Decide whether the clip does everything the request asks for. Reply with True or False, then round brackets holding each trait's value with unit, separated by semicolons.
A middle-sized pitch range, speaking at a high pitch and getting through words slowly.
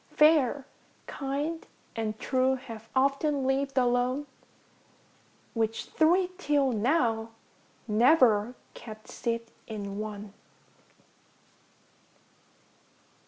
True (3.9 semitones; 255 Hz; 75 wpm)